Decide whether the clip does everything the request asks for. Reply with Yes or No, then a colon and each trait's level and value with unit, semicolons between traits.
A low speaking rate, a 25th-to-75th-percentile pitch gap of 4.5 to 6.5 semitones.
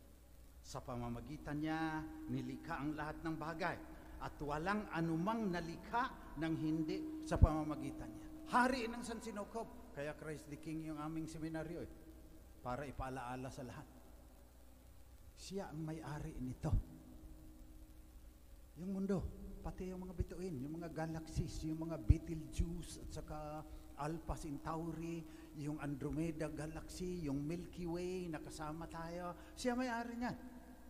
No: slow, 125 wpm; average, 4.1 semitones